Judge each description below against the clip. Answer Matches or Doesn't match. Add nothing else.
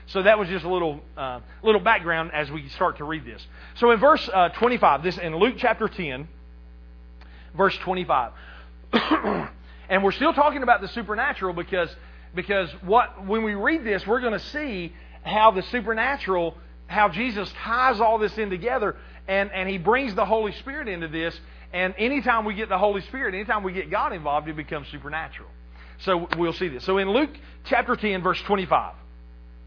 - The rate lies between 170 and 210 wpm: Matches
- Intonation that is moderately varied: Doesn't match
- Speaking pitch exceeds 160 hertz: Matches